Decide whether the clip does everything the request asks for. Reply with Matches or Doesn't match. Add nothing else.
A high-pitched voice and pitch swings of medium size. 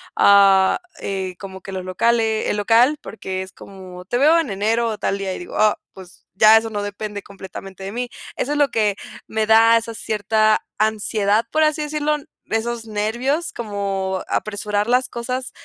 Matches